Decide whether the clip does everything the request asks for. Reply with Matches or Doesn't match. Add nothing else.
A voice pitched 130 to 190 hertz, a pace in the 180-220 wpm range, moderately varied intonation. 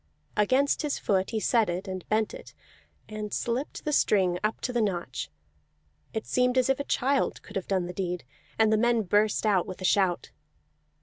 Doesn't match